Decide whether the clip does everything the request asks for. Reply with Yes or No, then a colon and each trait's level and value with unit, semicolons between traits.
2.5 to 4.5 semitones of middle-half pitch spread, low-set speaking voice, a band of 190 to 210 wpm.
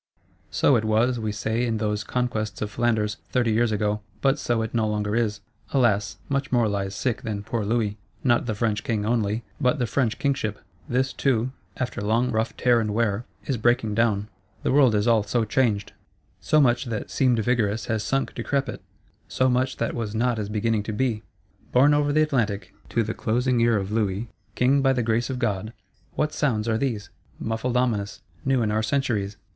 Yes: average, 2.9 semitones; low, 115 Hz; average, 195 wpm